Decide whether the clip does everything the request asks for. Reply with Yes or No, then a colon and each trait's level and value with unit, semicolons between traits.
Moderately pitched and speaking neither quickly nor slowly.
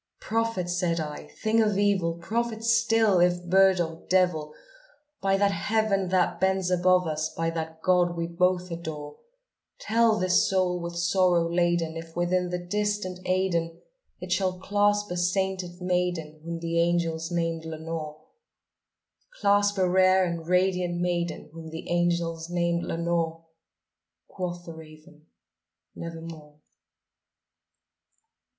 No: medium, 175 Hz; slow, 130 wpm